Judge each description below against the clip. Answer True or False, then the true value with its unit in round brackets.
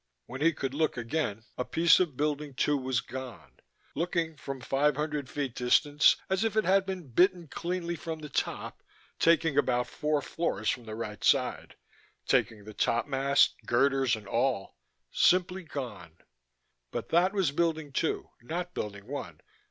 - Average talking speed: True (160 wpm)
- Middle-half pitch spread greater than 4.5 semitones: True (5.1 semitones)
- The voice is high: False (145 Hz)